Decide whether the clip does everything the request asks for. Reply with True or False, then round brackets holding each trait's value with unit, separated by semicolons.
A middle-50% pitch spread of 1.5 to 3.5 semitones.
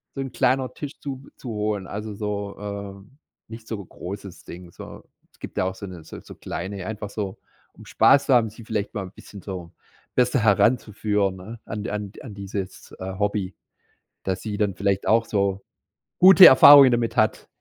True (2.7 semitones)